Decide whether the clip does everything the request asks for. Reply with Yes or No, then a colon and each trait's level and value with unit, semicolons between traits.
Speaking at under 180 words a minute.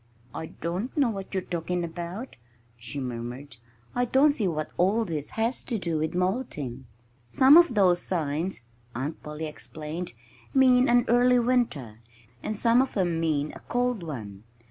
Yes: average, 160 wpm